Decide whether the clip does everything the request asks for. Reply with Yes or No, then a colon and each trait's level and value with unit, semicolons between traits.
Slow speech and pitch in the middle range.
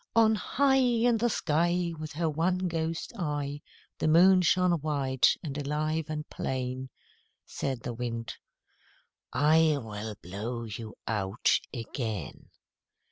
Yes: slow, 125 wpm; medium, 150 Hz